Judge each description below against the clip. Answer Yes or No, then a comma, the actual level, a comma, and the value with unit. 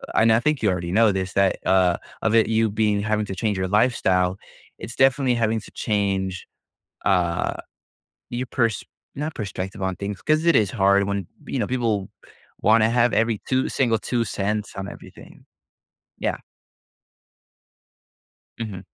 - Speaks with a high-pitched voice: No, low, 105 Hz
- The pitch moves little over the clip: No, average, 3.1 semitones